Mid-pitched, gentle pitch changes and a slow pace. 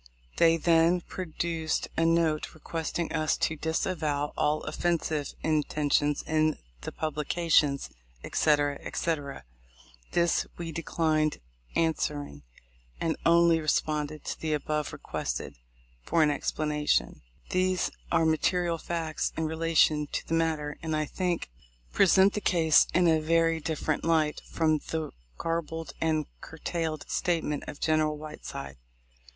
Yes: medium, 160 Hz; narrow, 1.6 semitones; slow, 125 wpm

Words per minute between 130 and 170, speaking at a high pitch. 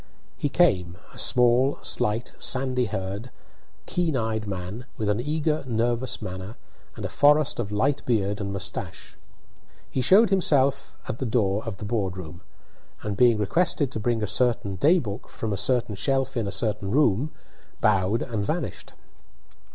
No: average, 165 wpm; low, 115 Hz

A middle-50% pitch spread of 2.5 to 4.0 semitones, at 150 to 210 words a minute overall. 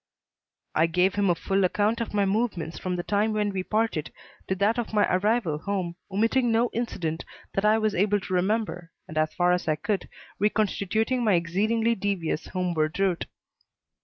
Yes: average, 3.4 semitones; average, 180 wpm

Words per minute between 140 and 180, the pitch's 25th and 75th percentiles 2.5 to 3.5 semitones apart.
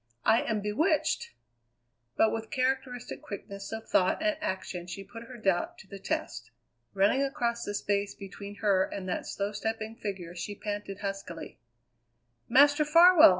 No: average, 150 wpm; average, 3.9 semitones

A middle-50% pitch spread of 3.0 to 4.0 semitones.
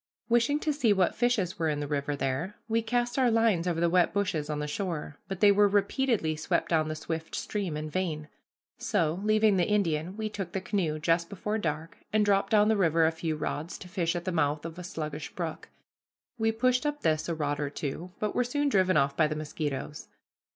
No: average, 5.3 semitones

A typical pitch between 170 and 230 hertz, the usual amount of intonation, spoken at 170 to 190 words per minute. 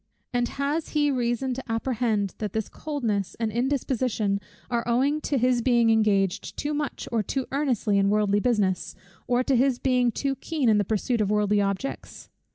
No: high, 240 Hz; average, 4.0 semitones; average, 175 wpm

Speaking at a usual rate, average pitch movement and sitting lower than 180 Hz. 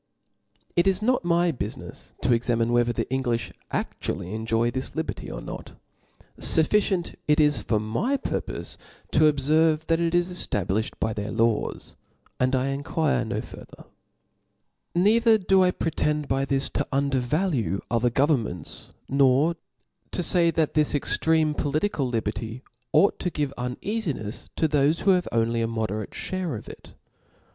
No: average, 155 wpm; wide, 6.3 semitones; medium, 140 Hz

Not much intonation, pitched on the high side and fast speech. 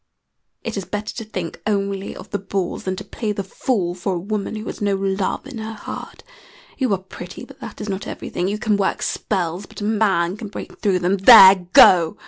Yes: narrow, 2.1 semitones; high, 200 Hz; fast, 220 wpm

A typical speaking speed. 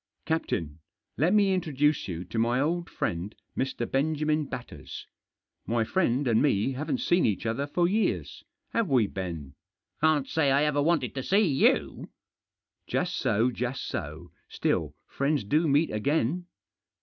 Yes: average, 160 wpm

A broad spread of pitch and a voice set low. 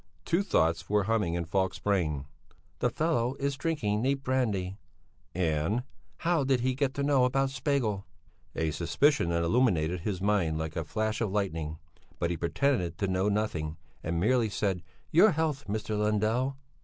Yes: wide, 7.3 semitones; low, 105 Hz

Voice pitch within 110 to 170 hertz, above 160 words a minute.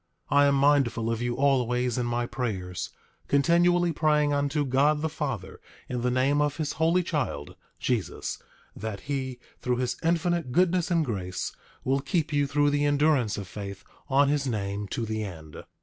Yes: low, 135 Hz; average, 175 wpm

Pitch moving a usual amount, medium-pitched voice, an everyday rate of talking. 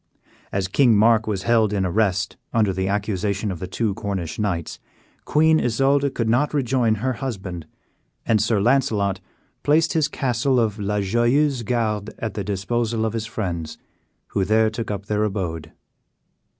No: average, 3.3 semitones; low, 110 Hz; average, 160 wpm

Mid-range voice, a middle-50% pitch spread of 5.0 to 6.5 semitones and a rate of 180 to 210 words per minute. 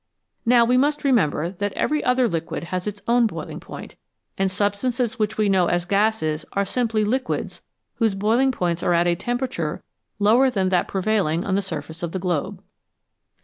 No: high, 205 Hz; average, 5.3 semitones; average, 185 wpm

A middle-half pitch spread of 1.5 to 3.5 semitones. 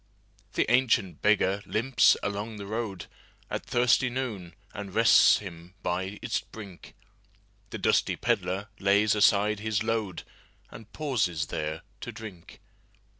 Yes: average, 3.1 semitones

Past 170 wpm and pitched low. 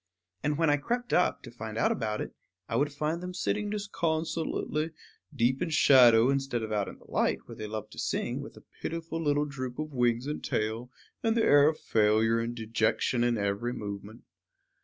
Yes: average, 200 wpm; low, 130 Hz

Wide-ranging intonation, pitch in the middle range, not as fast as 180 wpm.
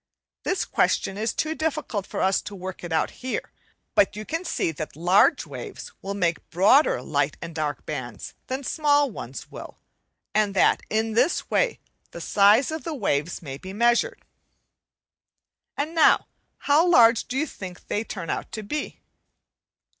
No: wide, 8.2 semitones; high, 210 Hz; average, 165 wpm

